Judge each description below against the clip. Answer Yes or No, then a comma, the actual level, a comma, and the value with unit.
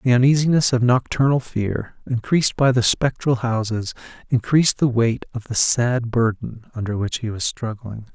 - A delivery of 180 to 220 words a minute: No, average, 160 wpm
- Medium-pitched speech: No, low, 120 Hz